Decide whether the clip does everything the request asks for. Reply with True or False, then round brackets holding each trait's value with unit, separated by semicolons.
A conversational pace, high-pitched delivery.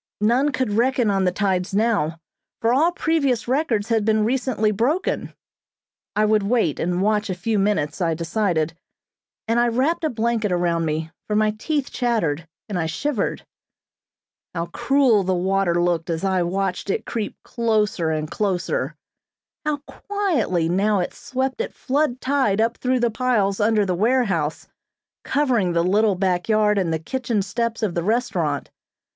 True (165 wpm; 210 Hz)